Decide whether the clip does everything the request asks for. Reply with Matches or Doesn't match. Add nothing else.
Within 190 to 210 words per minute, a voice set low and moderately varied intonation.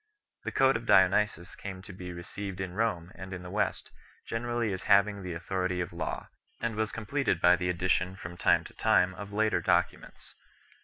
Matches